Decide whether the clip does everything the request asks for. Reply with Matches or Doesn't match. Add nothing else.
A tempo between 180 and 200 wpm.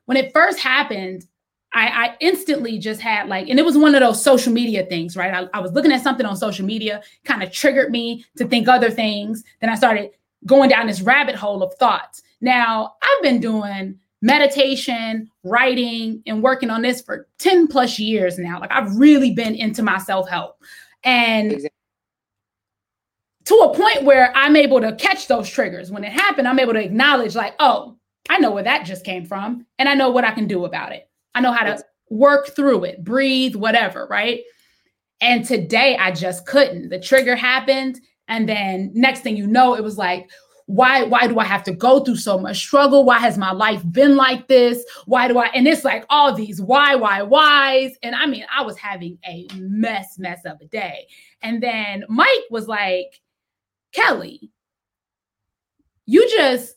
Matches